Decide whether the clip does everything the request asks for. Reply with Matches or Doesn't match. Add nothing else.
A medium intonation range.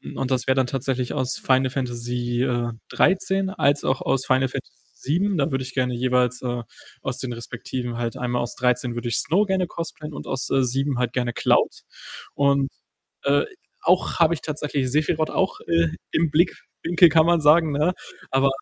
Matches